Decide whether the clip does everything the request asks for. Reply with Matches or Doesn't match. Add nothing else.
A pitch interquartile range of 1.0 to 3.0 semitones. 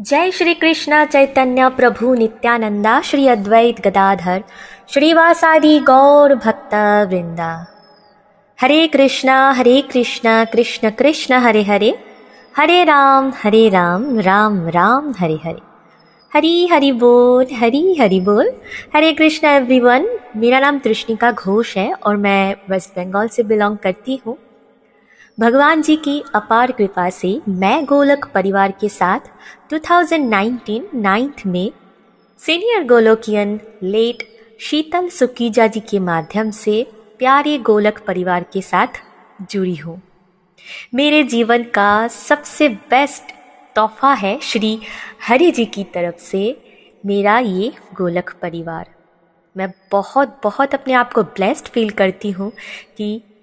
Doesn't match